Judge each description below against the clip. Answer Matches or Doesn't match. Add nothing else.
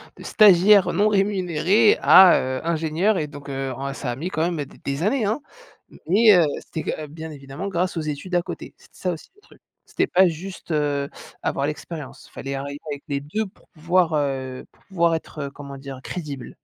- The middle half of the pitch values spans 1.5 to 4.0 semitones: Doesn't match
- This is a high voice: Doesn't match